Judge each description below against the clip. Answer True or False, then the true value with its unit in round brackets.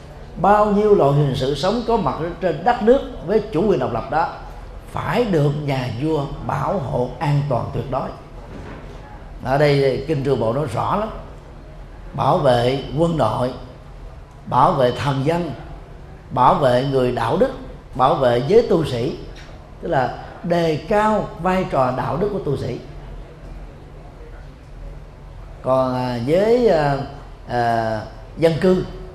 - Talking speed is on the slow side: True (145 wpm)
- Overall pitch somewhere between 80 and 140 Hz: True (135 Hz)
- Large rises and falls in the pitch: False (4.9 semitones)